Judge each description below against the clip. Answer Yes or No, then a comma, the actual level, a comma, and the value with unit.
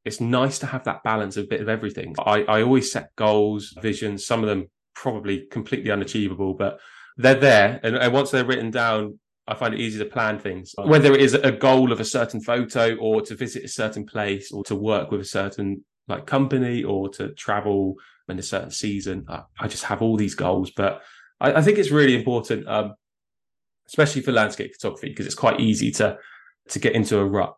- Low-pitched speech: Yes, low, 110 Hz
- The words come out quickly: Yes, fast, 215 wpm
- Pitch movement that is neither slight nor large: Yes, average, 4.3 semitones